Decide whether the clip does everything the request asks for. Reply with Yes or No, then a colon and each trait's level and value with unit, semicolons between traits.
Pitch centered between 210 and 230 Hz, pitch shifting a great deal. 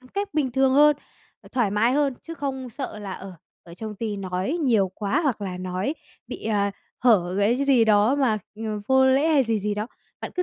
No: high, 225 Hz; average, 4.9 semitones